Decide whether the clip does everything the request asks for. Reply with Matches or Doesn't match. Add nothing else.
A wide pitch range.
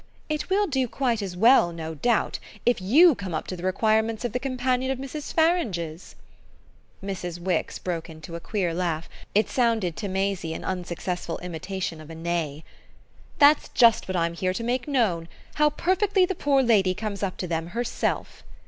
Matches